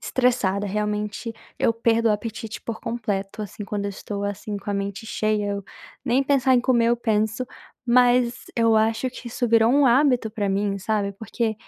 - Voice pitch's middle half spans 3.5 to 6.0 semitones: No, narrow, 2.6 semitones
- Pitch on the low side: No, high, 220 Hz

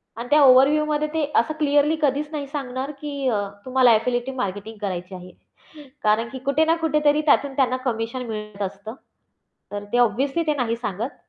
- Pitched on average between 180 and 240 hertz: No, very high, 255 Hz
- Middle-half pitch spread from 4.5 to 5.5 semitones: Yes, average, 4.8 semitones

